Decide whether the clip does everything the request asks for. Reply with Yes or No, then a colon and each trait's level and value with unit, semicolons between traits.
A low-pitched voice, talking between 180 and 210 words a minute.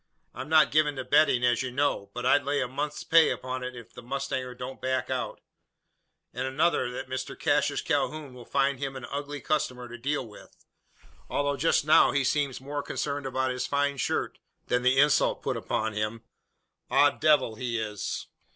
Yes: low, 130 Hz; average, 185 wpm